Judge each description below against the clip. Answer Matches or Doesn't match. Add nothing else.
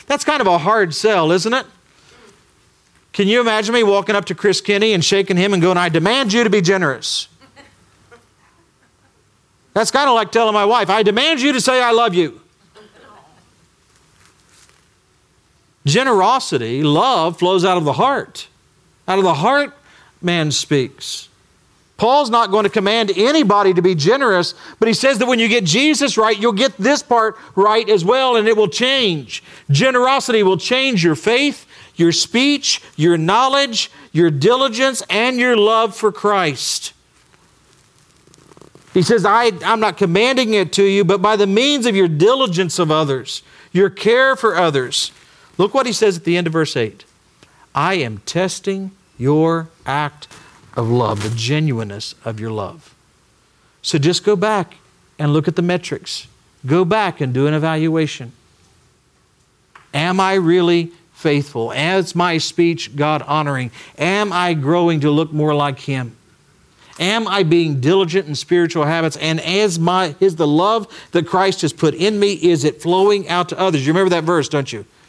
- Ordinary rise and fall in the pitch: Doesn't match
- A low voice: Doesn't match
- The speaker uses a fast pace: Doesn't match